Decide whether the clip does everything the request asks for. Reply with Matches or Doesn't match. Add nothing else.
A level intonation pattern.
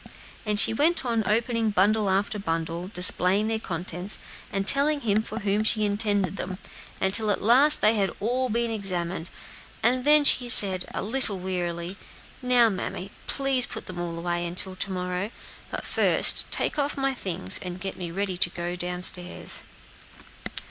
Doesn't match